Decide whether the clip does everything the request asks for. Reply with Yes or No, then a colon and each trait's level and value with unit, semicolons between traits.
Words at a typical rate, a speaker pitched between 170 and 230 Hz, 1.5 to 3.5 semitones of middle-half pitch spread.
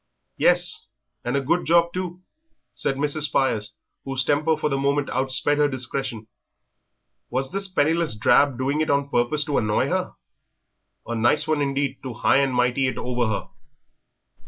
No: average, 160 wpm; medium, 140 Hz; average, 3.1 semitones